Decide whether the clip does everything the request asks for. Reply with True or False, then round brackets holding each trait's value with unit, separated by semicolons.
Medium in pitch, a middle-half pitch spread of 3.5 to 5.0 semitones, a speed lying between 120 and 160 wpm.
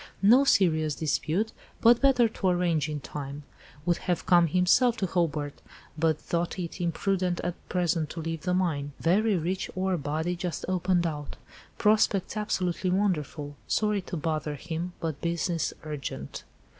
False (175 Hz; 3.1 semitones; 150 wpm)